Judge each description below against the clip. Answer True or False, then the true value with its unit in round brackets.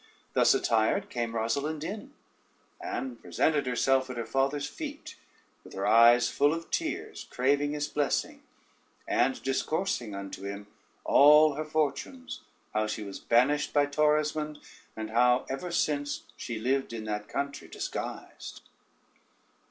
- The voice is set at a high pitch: False (140 Hz)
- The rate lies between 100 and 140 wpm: True (135 wpm)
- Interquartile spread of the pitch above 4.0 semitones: True (4.6 semitones)